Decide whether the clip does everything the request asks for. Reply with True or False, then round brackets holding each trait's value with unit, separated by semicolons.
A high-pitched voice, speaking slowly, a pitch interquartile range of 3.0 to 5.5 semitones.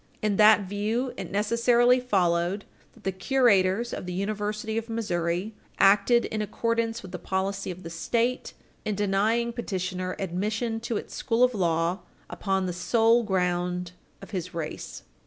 False (205 Hz; 155 wpm; 3.9 semitones)